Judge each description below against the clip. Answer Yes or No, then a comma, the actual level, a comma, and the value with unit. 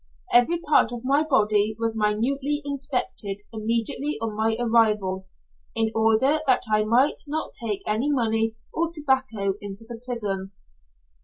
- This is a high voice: Yes, high, 225 Hz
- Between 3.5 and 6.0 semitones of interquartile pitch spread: Yes, average, 4.1 semitones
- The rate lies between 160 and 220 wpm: No, average, 140 wpm